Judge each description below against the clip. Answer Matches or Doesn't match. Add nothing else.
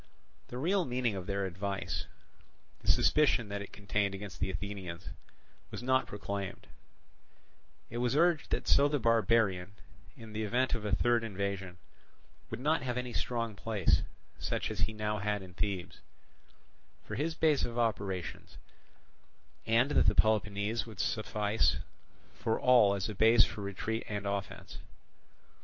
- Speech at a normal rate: Matches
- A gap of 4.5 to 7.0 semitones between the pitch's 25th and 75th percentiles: Doesn't match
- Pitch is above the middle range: Doesn't match